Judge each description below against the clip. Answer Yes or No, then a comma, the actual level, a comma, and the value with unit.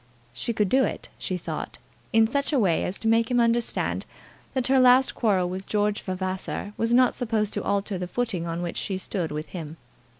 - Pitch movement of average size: Yes, average, 4.5 semitones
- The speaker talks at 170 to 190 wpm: No, fast, 205 wpm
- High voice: Yes, high, 210 Hz